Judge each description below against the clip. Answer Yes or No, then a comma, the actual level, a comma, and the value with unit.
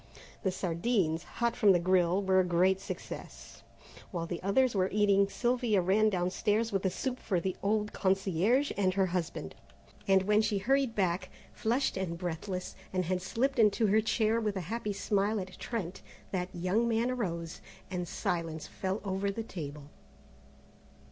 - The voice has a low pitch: No, high, 195 Hz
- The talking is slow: No, average, 165 wpm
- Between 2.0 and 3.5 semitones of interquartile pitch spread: Yes, average, 3.2 semitones